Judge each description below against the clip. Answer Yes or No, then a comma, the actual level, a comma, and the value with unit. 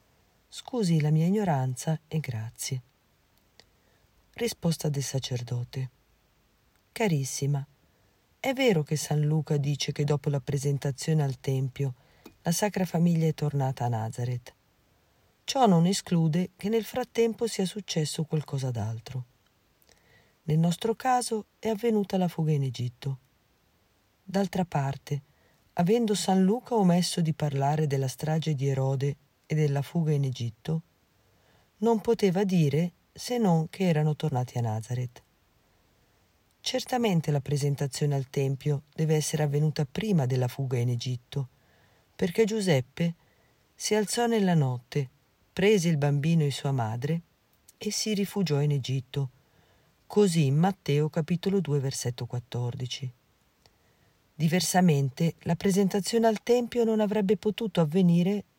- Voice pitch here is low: No, medium, 155 Hz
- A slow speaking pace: No, average, 125 wpm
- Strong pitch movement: Yes, wide, 5.9 semitones